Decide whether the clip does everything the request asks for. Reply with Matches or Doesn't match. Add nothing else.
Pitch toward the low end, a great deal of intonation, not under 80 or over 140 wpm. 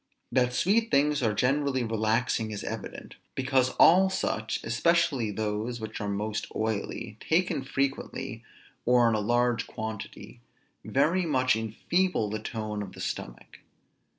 Doesn't match